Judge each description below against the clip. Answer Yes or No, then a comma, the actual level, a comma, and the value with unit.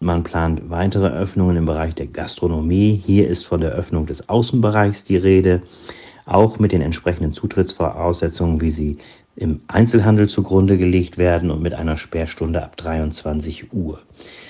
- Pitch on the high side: No, very low, 85 Hz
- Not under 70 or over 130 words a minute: No, average, 150 wpm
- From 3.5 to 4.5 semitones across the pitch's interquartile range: No, average, 3.1 semitones